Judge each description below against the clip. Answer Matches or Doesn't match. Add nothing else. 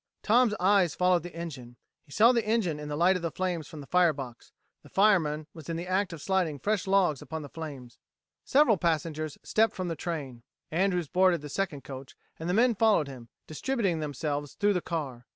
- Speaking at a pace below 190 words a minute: Doesn't match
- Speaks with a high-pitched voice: Doesn't match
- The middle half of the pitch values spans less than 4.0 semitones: Doesn't match